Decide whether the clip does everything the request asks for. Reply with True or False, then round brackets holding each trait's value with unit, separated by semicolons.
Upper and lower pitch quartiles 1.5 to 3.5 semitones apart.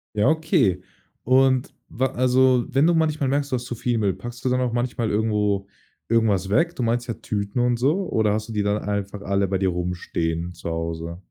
False (4.5 semitones)